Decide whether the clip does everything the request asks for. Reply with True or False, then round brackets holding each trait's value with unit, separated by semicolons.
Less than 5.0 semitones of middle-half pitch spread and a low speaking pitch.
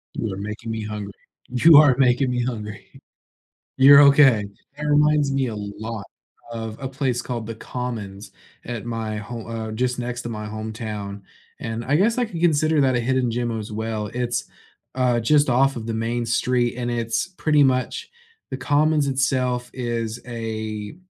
True (3.2 semitones; 120 Hz)